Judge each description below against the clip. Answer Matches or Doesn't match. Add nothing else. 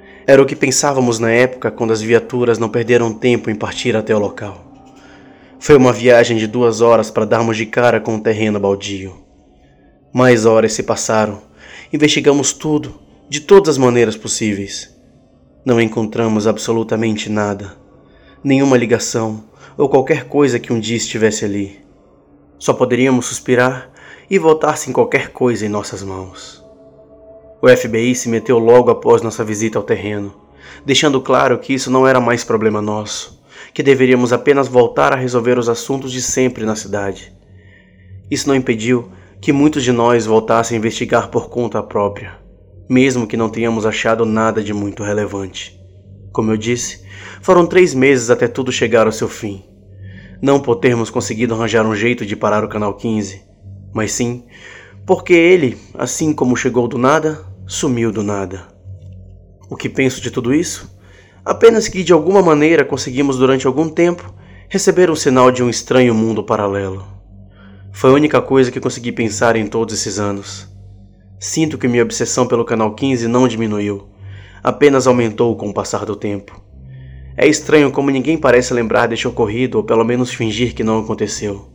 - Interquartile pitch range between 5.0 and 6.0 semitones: Doesn't match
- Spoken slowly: Doesn't match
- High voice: Doesn't match